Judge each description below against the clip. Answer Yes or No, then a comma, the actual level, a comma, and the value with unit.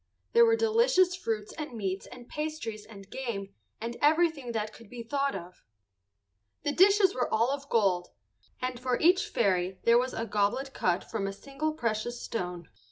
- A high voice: Yes, high, 240 Hz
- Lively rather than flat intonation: Yes, wide, 6.5 semitones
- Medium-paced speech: Yes, average, 170 wpm